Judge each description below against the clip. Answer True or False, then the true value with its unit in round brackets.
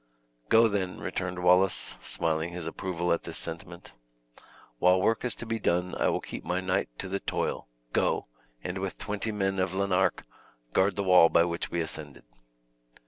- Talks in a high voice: False (90 Hz)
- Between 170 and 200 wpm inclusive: True (175 wpm)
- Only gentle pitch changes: True (2.0 semitones)